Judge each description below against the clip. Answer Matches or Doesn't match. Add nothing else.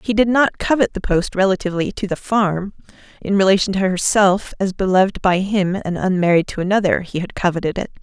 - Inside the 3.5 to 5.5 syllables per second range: Doesn't match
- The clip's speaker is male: Doesn't match